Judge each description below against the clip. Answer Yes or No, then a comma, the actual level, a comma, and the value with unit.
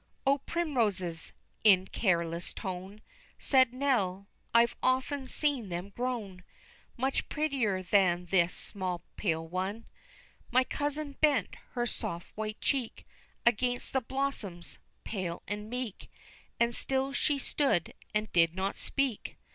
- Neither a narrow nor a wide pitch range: No, wide, 6.1 semitones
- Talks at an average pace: No, slow, 125 wpm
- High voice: Yes, high, 215 Hz